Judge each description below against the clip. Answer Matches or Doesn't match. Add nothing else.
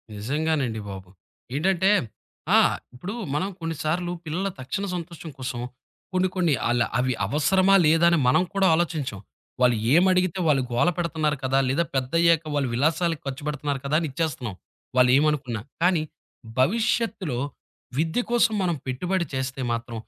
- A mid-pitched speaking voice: Matches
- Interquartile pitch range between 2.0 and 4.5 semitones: Doesn't match